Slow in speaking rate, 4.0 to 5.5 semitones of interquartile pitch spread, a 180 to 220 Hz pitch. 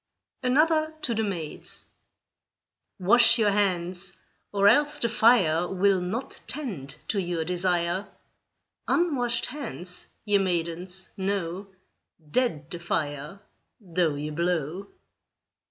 Yes: slow, 105 wpm; average, 5.1 semitones; high, 190 Hz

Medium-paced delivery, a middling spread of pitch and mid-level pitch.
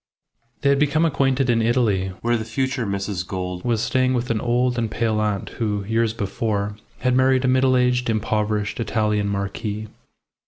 No: average, 170 wpm; average, 3.4 semitones; low, 115 Hz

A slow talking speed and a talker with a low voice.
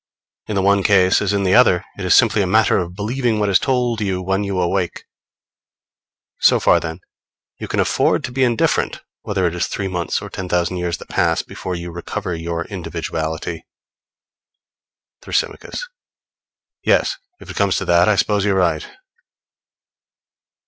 No: average, 170 wpm; very low, 95 Hz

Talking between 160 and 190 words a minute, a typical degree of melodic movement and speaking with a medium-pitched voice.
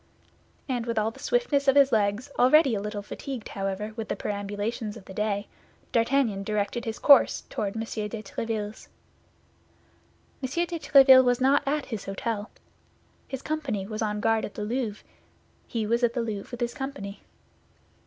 No: average, 170 wpm; average, 4.0 semitones; high, 225 Hz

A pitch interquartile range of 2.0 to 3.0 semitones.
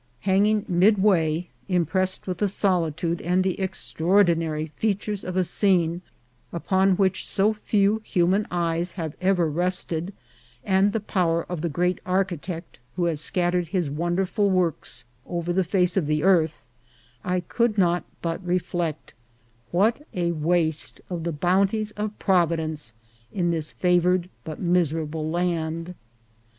Yes: narrow, 2.4 semitones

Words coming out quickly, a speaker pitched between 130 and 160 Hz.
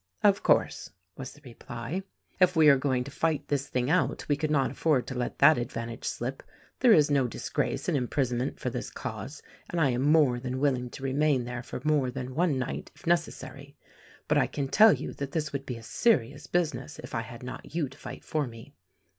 Yes: fast, 215 wpm; medium, 140 Hz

